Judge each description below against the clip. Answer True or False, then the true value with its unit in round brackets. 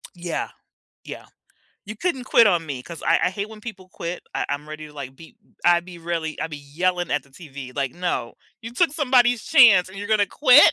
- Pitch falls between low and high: True (180 Hz)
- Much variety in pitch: True (5.9 semitones)